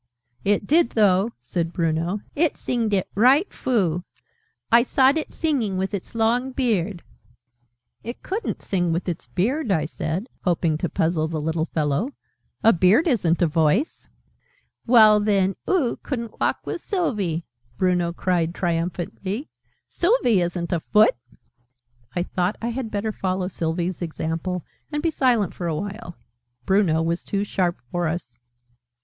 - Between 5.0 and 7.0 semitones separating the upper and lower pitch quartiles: Yes, wide, 5.4 semitones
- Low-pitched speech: No, high, 190 Hz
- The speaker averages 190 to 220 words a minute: No, average, 150 wpm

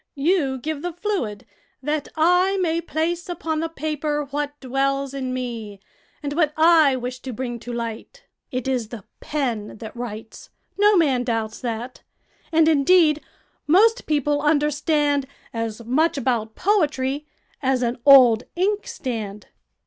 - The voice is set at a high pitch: Yes, very high, 280 Hz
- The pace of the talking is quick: No, average, 140 wpm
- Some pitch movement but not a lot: Yes, average, 4.5 semitones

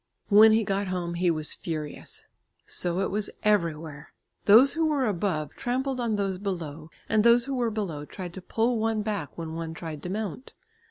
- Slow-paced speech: No, average, 185 wpm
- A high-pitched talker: Yes, high, 195 Hz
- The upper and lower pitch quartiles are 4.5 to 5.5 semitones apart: Yes, average, 5.1 semitones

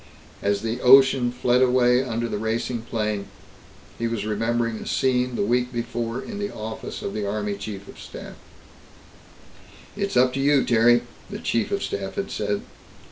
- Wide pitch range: No, average, 2.8 semitones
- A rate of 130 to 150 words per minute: No, average, 170 wpm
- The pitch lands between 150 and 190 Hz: No, low, 120 Hz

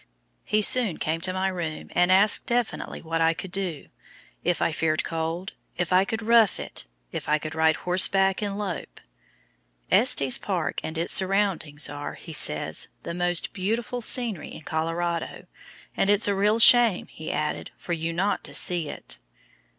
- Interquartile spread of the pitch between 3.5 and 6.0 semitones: Yes, average, 3.9 semitones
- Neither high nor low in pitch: Yes, medium, 180 Hz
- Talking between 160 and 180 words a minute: Yes, average, 170 wpm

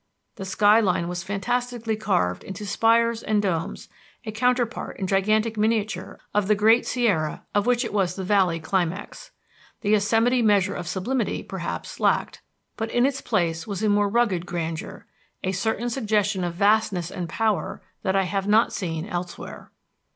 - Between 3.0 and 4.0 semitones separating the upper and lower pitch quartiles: Yes, average, 3.4 semitones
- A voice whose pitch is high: Yes, high, 205 Hz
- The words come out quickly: No, average, 165 wpm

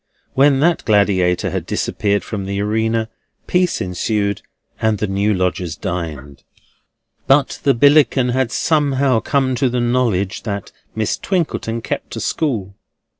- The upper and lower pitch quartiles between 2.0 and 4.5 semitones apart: No, average, 5.1 semitones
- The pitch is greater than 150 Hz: No, low, 110 Hz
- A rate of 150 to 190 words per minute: No, slow, 135 wpm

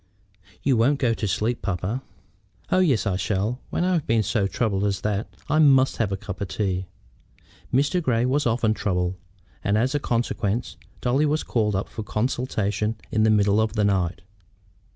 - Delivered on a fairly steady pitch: No, average, 4.1 semitones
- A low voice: Yes, low, 110 Hz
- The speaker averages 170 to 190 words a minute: Yes, average, 180 wpm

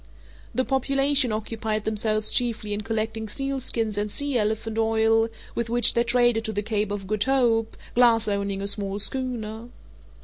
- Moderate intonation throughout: No, narrow, 2.2 semitones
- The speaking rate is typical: Yes, average, 160 wpm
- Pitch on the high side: Yes, high, 225 Hz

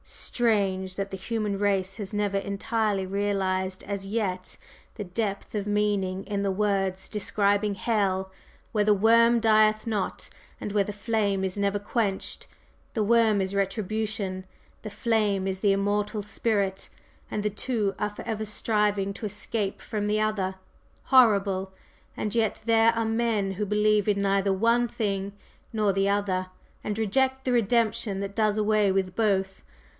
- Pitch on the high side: Yes, high, 205 Hz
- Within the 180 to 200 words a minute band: No, average, 155 wpm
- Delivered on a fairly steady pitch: Yes, narrow, 1.8 semitones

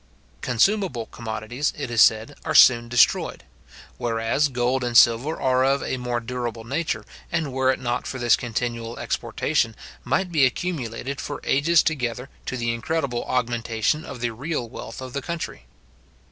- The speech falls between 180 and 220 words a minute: No, average, 160 wpm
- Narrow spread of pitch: No, average, 3.1 semitones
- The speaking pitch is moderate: No, low, 125 Hz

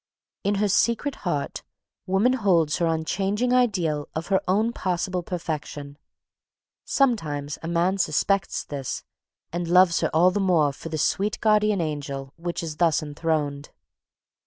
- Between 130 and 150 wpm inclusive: Yes, average, 140 wpm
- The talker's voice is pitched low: No, medium, 175 Hz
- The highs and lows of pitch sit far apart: No, average, 4.4 semitones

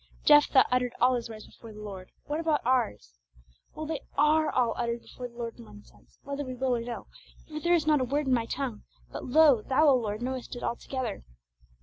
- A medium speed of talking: No, fast, 225 wpm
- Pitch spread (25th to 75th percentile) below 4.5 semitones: Yes, average, 3.9 semitones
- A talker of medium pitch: No, very high, 250 Hz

